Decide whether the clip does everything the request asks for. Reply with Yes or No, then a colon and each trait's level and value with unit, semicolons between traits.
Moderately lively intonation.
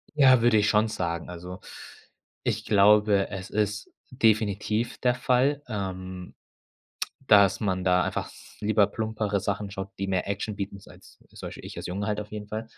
No: narrow, 2.0 semitones